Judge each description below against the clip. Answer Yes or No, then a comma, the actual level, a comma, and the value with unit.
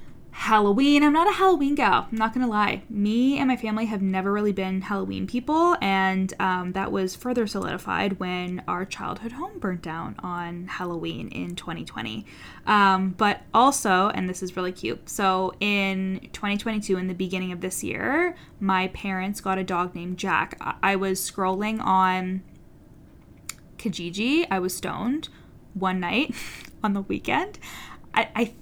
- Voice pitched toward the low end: No, high, 195 Hz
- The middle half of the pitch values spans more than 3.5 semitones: No, average, 3.2 semitones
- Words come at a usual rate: Yes, average, 160 wpm